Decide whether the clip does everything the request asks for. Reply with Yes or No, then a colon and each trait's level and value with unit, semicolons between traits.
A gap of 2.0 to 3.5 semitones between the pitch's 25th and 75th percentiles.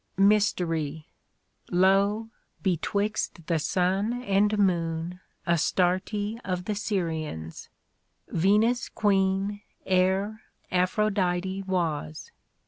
Yes: average, 2.9 semitones